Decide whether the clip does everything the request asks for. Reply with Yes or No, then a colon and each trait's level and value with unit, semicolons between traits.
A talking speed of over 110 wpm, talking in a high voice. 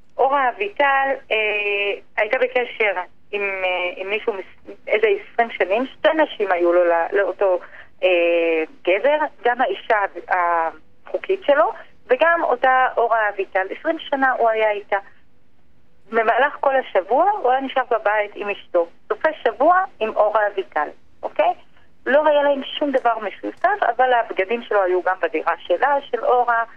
Yes: average, 140 wpm; high, 230 Hz